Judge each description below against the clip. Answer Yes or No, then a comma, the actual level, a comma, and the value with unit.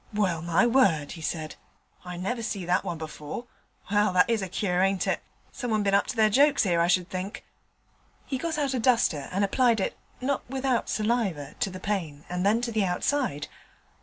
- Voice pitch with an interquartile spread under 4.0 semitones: No, average, 5.0 semitones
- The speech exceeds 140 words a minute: Yes, average, 200 wpm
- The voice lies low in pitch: No, high, 200 Hz